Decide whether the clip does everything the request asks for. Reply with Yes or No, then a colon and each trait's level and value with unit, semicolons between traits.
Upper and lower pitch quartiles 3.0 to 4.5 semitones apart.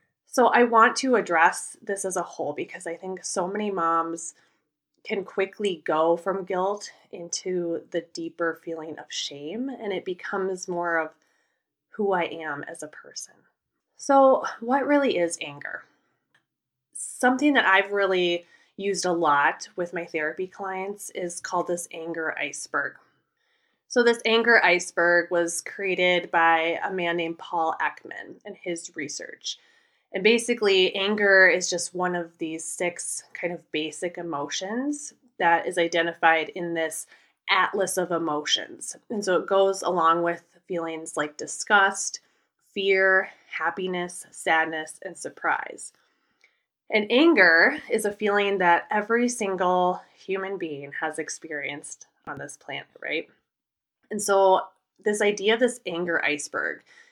Yes: average, 3.5 semitones